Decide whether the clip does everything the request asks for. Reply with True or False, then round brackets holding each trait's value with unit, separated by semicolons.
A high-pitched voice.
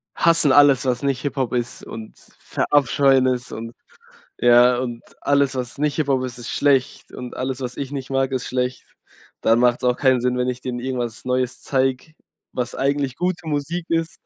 False (130 Hz)